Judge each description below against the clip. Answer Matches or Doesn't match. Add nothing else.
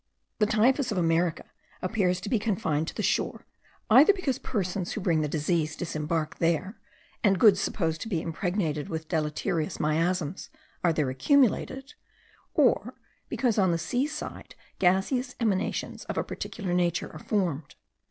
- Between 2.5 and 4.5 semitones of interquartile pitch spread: Doesn't match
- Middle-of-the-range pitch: Matches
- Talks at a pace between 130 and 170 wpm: Matches